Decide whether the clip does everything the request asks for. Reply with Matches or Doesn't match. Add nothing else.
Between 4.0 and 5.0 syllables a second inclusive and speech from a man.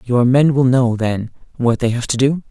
Matches